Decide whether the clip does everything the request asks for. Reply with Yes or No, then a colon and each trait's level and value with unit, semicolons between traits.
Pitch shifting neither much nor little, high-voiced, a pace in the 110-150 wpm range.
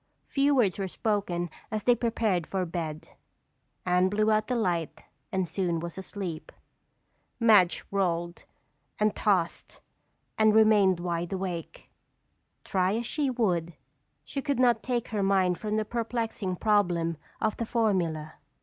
Yes: average, 4.0 semitones; high, 195 Hz; average, 140 wpm